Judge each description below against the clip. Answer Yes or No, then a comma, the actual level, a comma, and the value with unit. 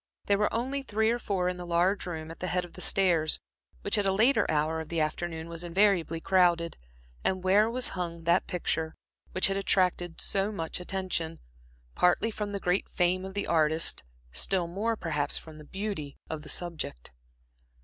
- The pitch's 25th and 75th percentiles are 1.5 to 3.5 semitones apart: Yes, average, 3.2 semitones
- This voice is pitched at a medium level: Yes, medium, 180 Hz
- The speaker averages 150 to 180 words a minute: No, average, 190 wpm